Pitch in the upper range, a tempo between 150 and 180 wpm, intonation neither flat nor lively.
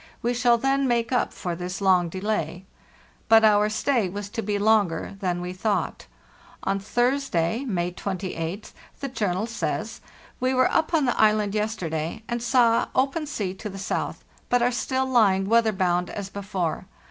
Yes: high, 210 Hz; average, 170 wpm; average, 4.4 semitones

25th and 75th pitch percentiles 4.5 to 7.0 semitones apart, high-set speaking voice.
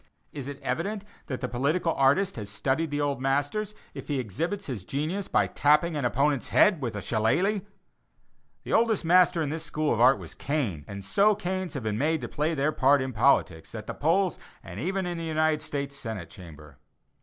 No: wide, 5.6 semitones; medium, 145 Hz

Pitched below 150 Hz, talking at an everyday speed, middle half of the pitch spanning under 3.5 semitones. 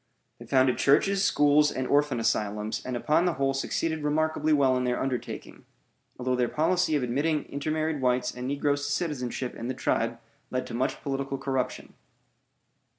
Yes: low, 135 Hz; average, 165 wpm; average, 3.0 semitones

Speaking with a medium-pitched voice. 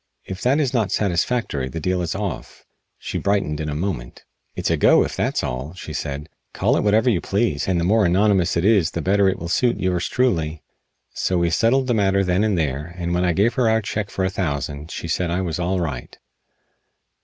No: very low, 90 Hz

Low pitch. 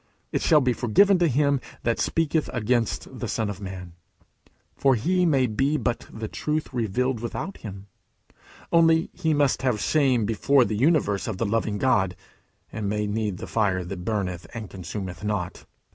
Yes: low, 115 Hz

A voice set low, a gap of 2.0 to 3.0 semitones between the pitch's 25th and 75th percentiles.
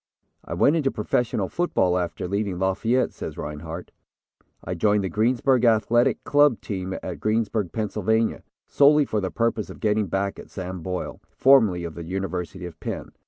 No: low, 105 Hz; average, 4.0 semitones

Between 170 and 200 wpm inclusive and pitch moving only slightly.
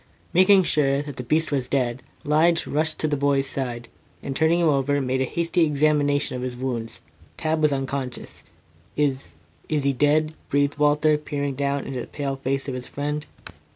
Yes: average, 185 wpm; narrow, 2.2 semitones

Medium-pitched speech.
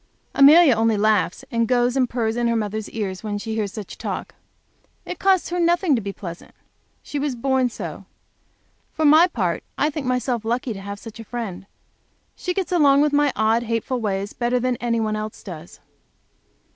No: high, 235 Hz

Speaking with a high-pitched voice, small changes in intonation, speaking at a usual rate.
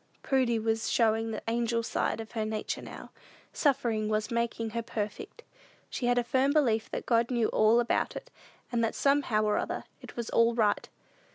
Yes: high, 230 Hz; narrow, 1.7 semitones; average, 185 wpm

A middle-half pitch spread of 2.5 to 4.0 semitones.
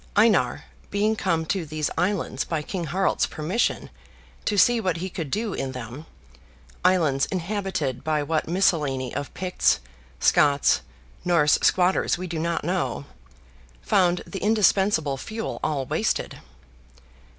No: average, 4.4 semitones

